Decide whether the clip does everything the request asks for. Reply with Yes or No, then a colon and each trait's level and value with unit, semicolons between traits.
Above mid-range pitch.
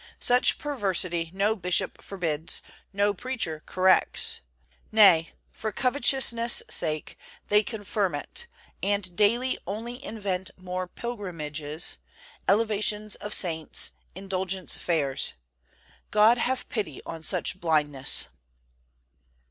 Yes: high, 195 Hz